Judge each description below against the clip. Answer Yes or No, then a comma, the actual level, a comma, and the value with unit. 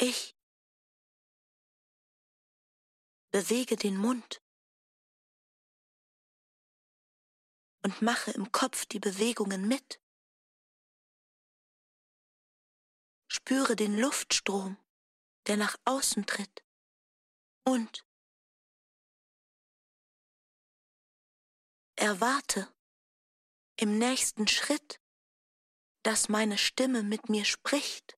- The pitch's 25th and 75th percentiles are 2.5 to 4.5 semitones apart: Yes, average, 3.4 semitones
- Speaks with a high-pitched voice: Yes, high, 225 Hz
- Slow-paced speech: Yes, slow, 60 wpm